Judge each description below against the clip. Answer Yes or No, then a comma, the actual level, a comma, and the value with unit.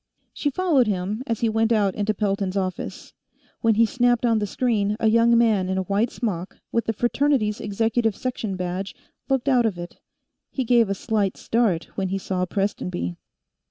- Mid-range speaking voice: No, high, 215 Hz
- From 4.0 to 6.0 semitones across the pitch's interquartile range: No, average, 3.3 semitones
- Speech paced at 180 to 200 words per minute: Yes, average, 185 wpm